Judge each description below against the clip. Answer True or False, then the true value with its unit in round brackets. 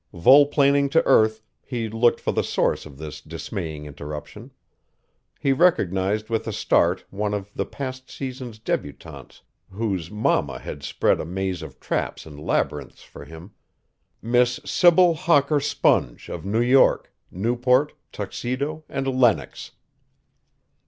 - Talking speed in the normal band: False (130 wpm)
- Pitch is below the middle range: True (115 Hz)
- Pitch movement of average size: False (6.3 semitones)